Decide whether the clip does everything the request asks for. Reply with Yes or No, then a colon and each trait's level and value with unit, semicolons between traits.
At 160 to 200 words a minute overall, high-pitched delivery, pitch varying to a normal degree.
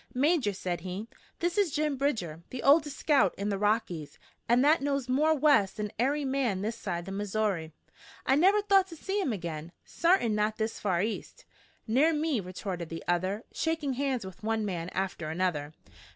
No: average, 180 wpm; high, 220 Hz; wide, 7.6 semitones